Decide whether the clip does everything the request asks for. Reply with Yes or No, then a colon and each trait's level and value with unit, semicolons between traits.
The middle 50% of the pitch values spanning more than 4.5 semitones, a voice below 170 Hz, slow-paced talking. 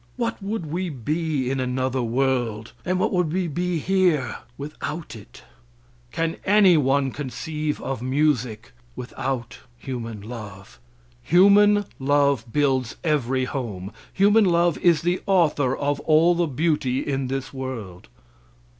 Yes: average, 5.2 semitones; medium, 140 Hz; slow, 130 wpm